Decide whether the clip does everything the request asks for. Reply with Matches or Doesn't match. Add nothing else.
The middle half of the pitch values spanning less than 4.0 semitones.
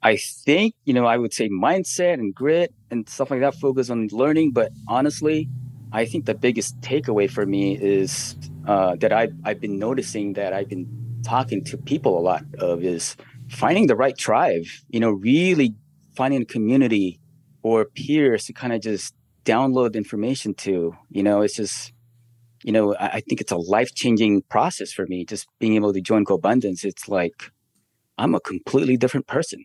Doesn't match